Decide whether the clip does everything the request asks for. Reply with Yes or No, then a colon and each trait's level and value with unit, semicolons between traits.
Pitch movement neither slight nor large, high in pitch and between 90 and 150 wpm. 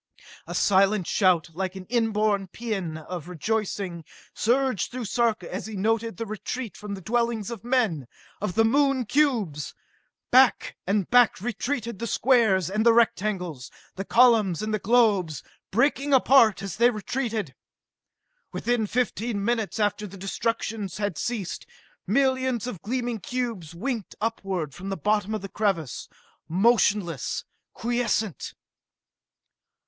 Yes: average, 3.8 semitones; high, 215 Hz; slow, 135 wpm